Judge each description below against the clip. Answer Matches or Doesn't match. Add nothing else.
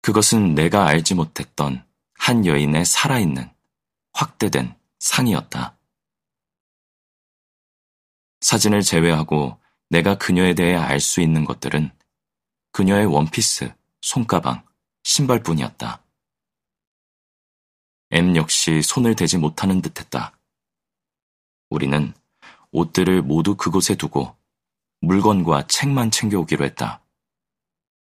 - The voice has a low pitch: Matches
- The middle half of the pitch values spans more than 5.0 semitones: Matches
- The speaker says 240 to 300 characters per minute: Doesn't match